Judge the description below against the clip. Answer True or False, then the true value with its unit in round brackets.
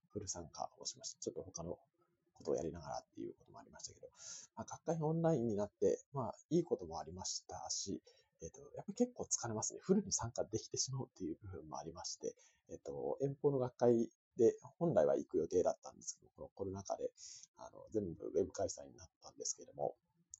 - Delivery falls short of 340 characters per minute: False (450 characters per minute)